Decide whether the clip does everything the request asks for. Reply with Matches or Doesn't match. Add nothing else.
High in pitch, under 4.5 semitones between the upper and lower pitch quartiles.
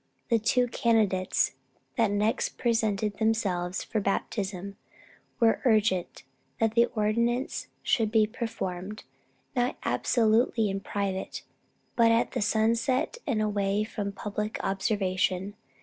Matches